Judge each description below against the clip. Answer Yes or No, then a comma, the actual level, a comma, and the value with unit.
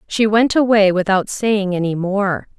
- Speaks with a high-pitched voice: Yes, high, 200 Hz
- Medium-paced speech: Yes, average, 165 wpm